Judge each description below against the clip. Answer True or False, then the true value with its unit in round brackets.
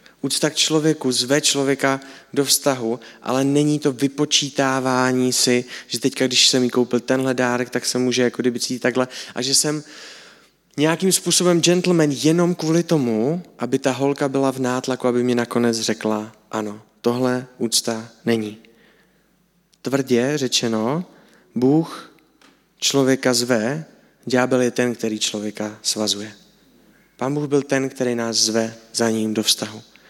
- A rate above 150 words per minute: False (145 wpm)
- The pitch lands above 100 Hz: True (125 Hz)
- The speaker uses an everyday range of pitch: True (3.3 semitones)